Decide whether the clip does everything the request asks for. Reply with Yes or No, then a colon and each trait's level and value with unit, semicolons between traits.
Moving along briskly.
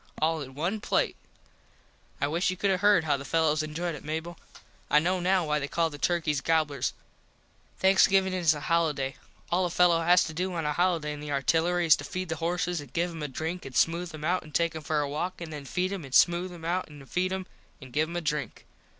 Yes: fast, 245 wpm